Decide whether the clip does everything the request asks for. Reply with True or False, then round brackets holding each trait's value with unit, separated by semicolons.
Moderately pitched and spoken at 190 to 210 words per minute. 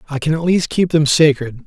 False (155 Hz; 255 wpm)